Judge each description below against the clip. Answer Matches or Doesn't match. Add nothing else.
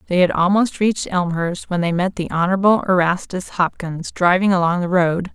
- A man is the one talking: Doesn't match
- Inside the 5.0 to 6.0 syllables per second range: Matches